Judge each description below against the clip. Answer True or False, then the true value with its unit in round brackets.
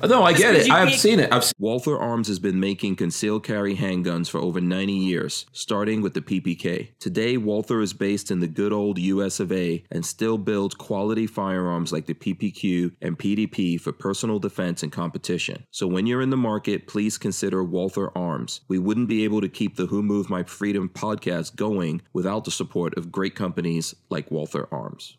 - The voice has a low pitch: True (100 Hz)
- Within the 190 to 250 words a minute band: True (200 wpm)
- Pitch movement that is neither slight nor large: True (3.0 semitones)